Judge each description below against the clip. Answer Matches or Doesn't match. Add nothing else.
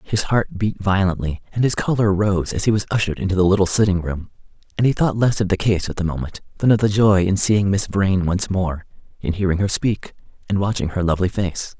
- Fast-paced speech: Matches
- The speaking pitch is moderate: Doesn't match